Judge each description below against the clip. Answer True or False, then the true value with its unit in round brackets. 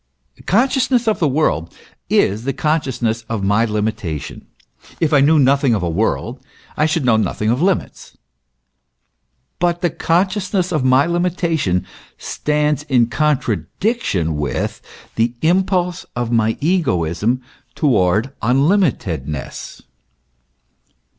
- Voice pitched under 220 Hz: True (135 Hz)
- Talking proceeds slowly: True (120 wpm)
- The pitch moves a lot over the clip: True (7.9 semitones)